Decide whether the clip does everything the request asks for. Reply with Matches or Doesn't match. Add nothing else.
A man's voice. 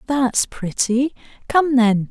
Doesn't match